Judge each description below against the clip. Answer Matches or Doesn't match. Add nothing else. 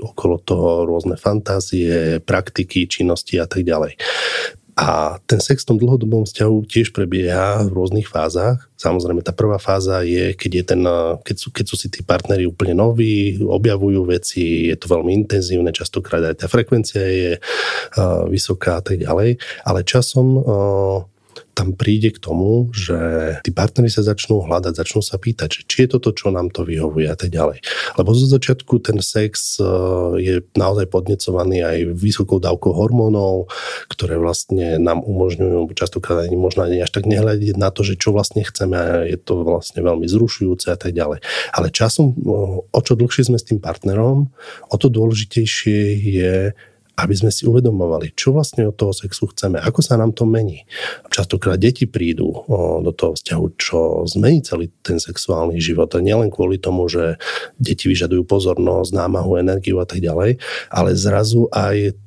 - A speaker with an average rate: Doesn't match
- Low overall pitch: Matches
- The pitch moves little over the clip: Doesn't match